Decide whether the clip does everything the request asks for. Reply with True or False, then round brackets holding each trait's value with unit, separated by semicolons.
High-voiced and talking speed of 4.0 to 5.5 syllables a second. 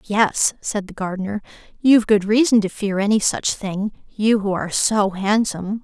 True (205 Hz; 4.9 syllables/s)